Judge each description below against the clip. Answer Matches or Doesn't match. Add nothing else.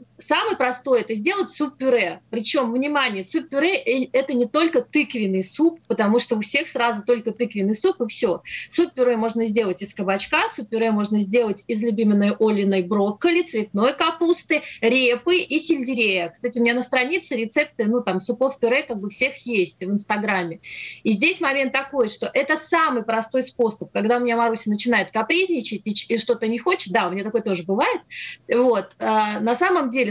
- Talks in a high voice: Matches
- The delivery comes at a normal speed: Doesn't match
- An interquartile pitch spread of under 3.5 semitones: Doesn't match